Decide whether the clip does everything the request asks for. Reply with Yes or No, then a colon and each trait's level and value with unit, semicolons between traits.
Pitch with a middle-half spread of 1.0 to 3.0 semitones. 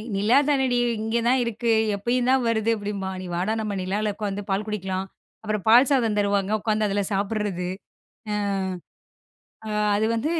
Yes: narrow, 2.6 semitones